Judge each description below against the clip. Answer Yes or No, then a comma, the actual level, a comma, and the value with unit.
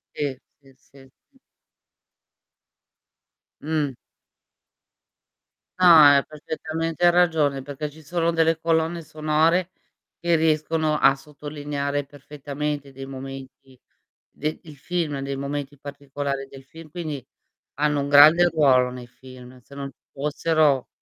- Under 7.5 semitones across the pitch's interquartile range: Yes, narrow, 2.4 semitones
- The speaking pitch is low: No, medium, 145 Hz